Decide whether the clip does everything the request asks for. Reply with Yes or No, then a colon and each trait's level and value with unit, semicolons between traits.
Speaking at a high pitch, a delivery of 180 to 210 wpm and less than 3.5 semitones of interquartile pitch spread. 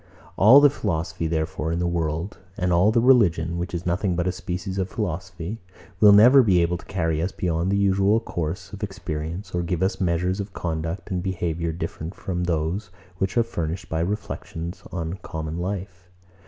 No: very low, 90 Hz; average, 185 wpm; average, 2.8 semitones